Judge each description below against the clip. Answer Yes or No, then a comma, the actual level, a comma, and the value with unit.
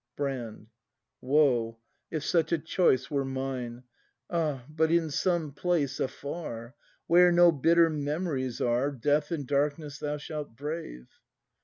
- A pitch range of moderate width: Yes, average, 3.7 semitones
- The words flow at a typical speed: No, slow, 130 wpm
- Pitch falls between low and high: Yes, medium, 145 Hz